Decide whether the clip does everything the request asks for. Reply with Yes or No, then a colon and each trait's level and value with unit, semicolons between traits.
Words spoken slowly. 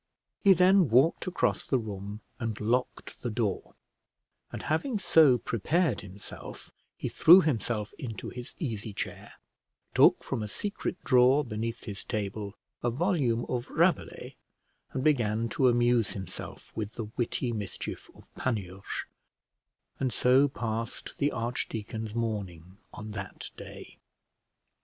Yes: slow, 130 wpm